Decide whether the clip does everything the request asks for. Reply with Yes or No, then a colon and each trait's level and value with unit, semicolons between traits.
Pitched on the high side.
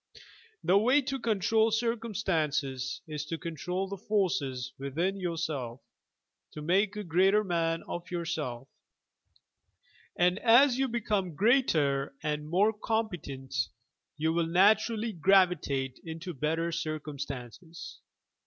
No: medium, 175 Hz